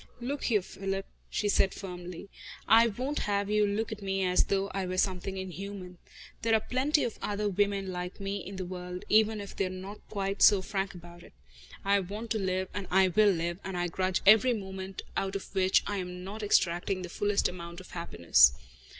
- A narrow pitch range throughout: Yes, narrow, 2.1 semitones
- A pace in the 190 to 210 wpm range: Yes, fast, 205 wpm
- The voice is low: No, high, 195 Hz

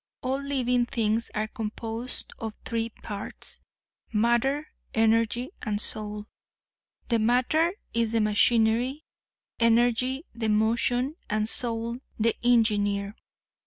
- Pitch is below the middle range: No, high, 230 Hz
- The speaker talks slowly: Yes, slow, 105 wpm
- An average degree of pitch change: No, narrow, 2.1 semitones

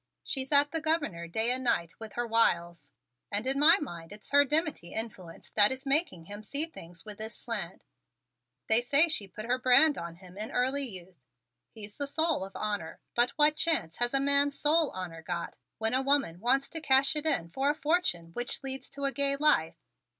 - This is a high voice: Yes, high, 245 Hz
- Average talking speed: No, fast, 210 wpm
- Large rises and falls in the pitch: Yes, wide, 7.2 semitones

